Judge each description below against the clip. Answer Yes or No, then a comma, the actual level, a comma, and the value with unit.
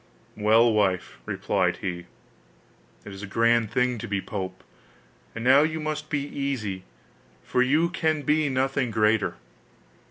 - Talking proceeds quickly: No, average, 145 wpm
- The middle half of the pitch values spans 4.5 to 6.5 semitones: Yes, wide, 5.5 semitones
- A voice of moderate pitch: No, low, 120 Hz